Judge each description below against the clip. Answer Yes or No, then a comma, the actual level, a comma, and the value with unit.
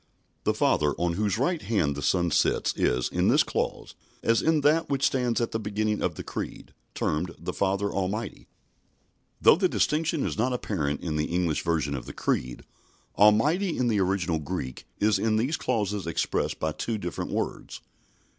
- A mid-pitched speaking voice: No, low, 100 Hz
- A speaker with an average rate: Yes, average, 180 wpm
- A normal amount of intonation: No, wide, 6.0 semitones